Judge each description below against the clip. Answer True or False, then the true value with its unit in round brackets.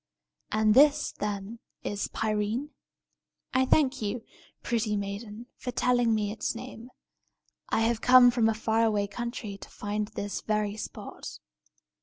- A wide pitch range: False (2.6 semitones)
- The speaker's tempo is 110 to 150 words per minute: True (140 wpm)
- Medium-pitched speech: False (220 Hz)